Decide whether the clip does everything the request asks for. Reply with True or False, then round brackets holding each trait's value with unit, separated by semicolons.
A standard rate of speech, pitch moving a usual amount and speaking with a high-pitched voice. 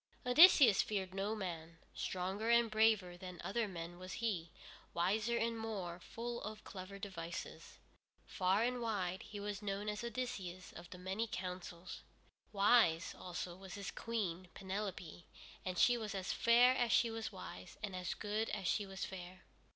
True (160 wpm; 3.6 semitones; 195 Hz)